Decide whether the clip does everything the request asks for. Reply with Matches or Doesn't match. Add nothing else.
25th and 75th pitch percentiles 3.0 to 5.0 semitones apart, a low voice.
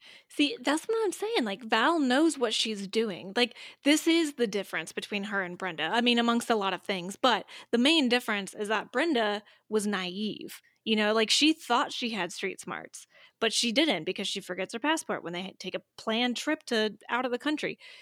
Doesn't match